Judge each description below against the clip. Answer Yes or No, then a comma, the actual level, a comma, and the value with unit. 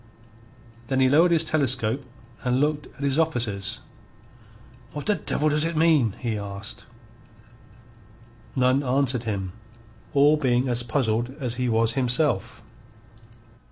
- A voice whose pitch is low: Yes, low, 130 Hz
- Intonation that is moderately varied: Yes, average, 4.1 semitones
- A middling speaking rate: No, slow, 125 wpm